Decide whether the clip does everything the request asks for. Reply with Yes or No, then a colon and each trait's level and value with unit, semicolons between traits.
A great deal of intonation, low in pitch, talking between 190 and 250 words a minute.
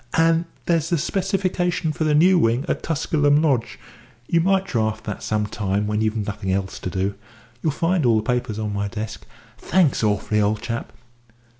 No: wide, 7.6 semitones; low, 120 Hz; average, 180 wpm